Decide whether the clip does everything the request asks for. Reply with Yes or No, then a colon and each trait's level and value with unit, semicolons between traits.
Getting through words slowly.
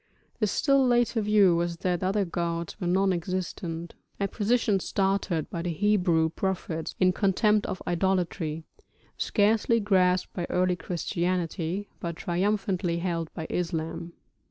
Yes: slow, 130 wpm